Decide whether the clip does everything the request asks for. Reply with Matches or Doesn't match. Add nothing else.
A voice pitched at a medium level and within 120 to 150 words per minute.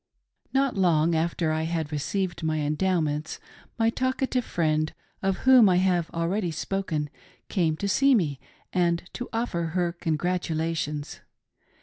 Matches